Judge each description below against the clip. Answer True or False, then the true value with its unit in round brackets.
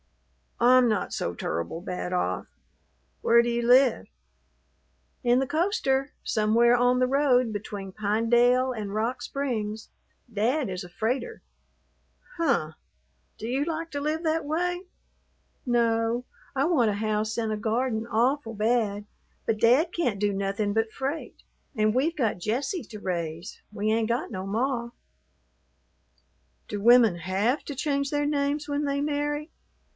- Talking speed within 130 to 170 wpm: True (145 wpm)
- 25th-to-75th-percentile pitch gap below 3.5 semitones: False (4.6 semitones)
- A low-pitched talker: False (235 Hz)